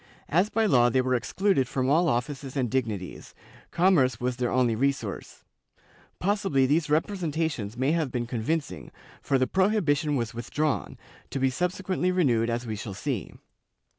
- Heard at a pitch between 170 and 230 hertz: No, low, 135 Hz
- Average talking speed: Yes, average, 155 wpm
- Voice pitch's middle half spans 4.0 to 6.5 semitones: Yes, average, 5.3 semitones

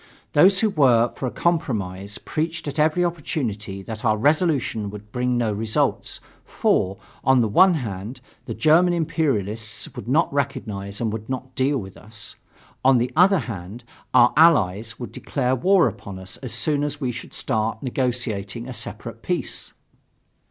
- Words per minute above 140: Yes, average, 160 wpm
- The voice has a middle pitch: No, low, 125 Hz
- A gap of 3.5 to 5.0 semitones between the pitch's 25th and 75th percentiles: No, wide, 5.6 semitones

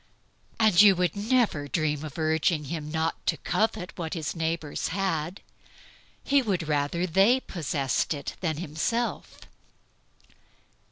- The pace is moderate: No, slow, 125 wpm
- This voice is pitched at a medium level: Yes, medium, 165 Hz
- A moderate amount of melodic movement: Yes, average, 4.0 semitones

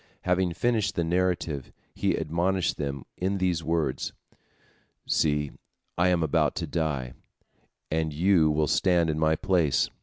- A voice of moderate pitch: No, very low, 80 Hz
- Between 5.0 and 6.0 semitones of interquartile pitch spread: No, average, 3.1 semitones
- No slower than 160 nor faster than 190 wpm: No, average, 140 wpm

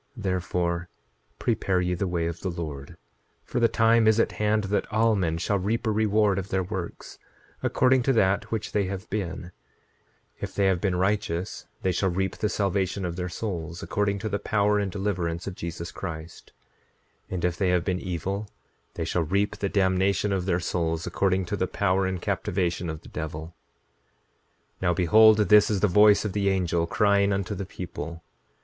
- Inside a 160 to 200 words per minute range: Yes, average, 190 wpm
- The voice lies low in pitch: Yes, very low, 95 Hz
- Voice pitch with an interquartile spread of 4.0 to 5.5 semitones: No, average, 2.7 semitones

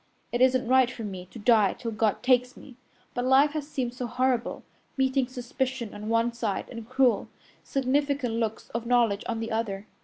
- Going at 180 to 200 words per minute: Yes, average, 185 wpm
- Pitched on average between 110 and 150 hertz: No, high, 245 Hz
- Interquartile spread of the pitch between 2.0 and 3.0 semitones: Yes, narrow, 2.5 semitones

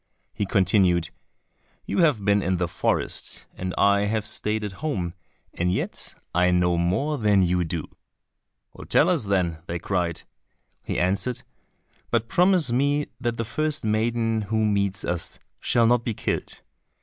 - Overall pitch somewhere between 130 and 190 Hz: No, low, 100 Hz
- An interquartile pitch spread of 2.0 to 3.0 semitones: No, average, 4.7 semitones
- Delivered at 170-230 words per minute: No, average, 150 wpm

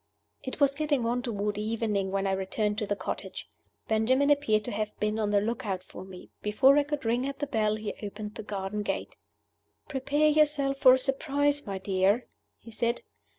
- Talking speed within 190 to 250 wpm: Yes, average, 195 wpm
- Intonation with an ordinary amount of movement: Yes, average, 4.9 semitones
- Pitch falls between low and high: No, high, 220 Hz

